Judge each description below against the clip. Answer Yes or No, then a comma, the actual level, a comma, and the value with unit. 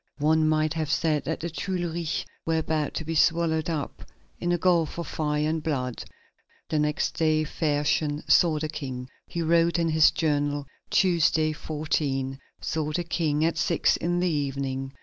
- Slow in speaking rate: No, average, 170 wpm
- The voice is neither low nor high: Yes, medium, 155 Hz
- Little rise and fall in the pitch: Yes, narrow, 1.8 semitones